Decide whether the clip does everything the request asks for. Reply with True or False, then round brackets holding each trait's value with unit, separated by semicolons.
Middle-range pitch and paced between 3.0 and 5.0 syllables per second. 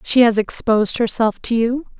False (230 Hz; 4.9 syllables/s)